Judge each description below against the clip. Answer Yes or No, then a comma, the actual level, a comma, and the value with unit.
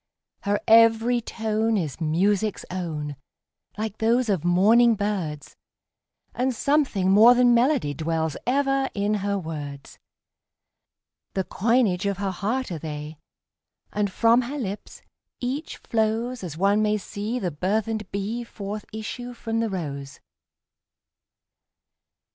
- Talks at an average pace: No, slow, 115 wpm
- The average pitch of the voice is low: No, high, 210 Hz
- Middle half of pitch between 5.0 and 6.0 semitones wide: No, average, 4.3 semitones